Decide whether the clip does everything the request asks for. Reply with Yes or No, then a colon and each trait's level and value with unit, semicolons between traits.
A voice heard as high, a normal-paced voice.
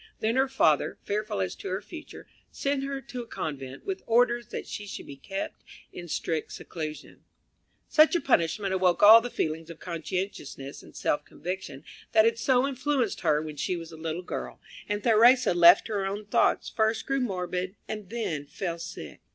Yes: high, 195 Hz; average, 185 wpm